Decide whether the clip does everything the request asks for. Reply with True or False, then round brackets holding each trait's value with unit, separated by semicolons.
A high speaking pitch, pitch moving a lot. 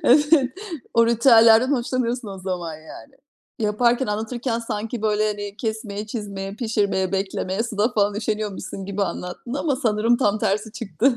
False (215 Hz; 2.9 semitones)